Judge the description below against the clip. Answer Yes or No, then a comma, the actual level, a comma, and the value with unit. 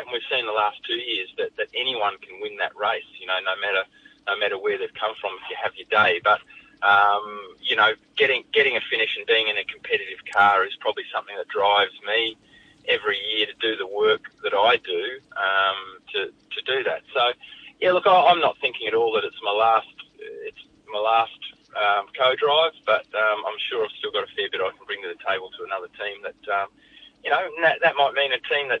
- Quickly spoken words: Yes, fast, 230 wpm